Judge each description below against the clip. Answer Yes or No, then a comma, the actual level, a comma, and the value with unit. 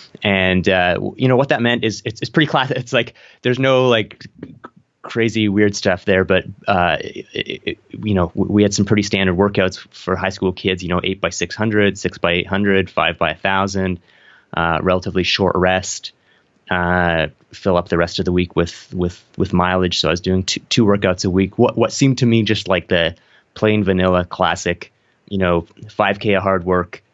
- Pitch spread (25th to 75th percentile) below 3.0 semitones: Yes, narrow, 2.6 semitones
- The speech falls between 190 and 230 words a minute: Yes, average, 200 wpm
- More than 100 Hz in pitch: No, very low, 95 Hz